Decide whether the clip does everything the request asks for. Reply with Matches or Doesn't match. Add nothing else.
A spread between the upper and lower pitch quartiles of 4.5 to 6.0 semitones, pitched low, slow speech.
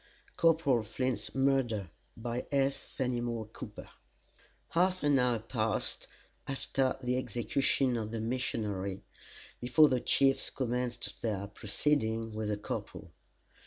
Doesn't match